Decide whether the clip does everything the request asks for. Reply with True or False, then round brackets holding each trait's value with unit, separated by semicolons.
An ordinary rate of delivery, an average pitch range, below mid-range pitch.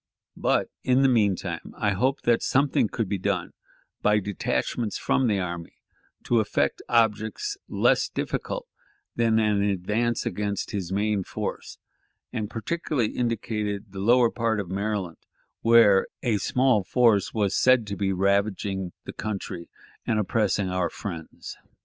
True (145 wpm; 3.0 semitones; 105 Hz)